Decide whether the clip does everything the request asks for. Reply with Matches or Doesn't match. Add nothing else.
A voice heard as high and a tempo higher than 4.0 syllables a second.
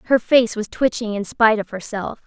Matches